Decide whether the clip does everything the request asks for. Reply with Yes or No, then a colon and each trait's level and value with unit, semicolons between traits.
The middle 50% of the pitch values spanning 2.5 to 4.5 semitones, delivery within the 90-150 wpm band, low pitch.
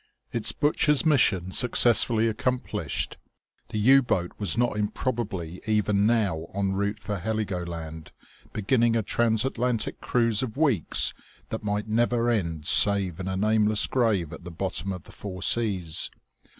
Yes: average, 3.9 semitones; average, 140 wpm; low, 105 Hz